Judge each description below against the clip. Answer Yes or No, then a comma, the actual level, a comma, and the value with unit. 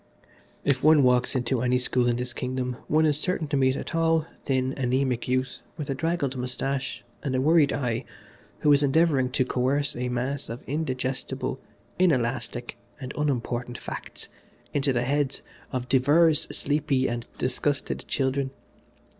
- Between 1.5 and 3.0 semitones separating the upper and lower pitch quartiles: Yes, narrow, 2.4 semitones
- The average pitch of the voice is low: Yes, low, 130 Hz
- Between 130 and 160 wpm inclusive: Yes, average, 155 wpm